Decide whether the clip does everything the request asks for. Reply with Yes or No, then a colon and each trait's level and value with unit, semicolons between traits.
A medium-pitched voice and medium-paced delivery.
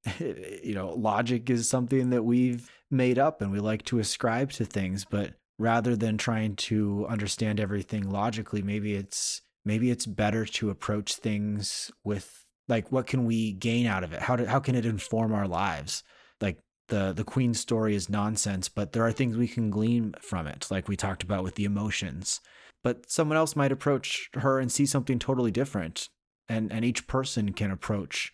No: low, 110 Hz; average, 190 wpm